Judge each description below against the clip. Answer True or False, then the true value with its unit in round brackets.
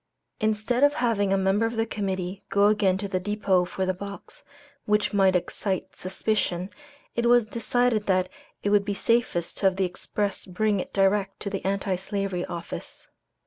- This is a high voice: True (200 Hz)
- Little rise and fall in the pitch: True (2.1 semitones)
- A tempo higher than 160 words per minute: True (180 wpm)